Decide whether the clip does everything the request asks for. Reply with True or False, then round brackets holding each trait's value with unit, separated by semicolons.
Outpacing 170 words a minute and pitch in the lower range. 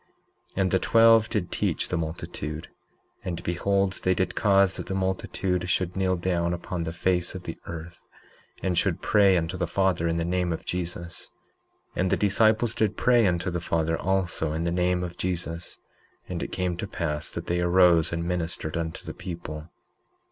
True (190 wpm; 90 Hz)